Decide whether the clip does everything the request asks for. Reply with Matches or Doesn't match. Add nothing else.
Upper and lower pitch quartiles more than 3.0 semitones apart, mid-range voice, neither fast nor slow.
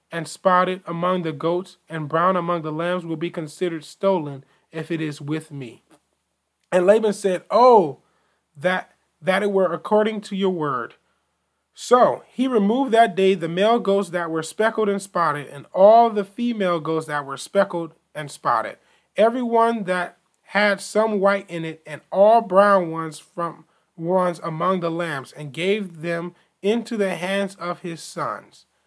Matches